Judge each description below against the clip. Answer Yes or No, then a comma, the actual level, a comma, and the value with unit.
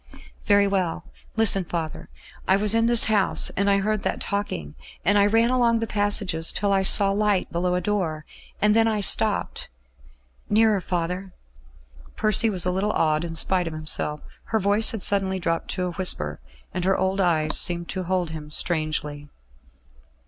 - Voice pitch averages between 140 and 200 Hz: Yes, high, 190 Hz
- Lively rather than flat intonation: No, average, 3.4 semitones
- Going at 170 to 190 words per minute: Yes, average, 175 wpm